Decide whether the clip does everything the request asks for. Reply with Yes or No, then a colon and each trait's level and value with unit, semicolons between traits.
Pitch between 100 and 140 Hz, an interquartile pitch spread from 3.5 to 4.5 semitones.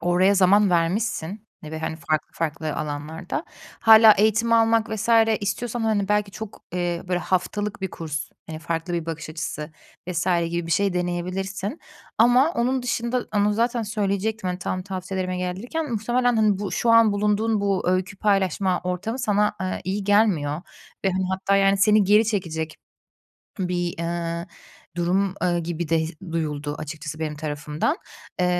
No: high, 190 Hz; average, 3.9 semitones